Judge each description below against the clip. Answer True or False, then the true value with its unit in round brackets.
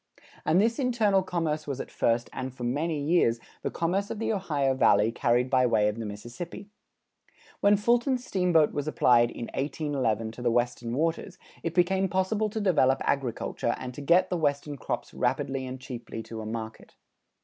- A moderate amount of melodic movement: False (7.1 semitones)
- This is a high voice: False (145 Hz)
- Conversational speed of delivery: True (180 wpm)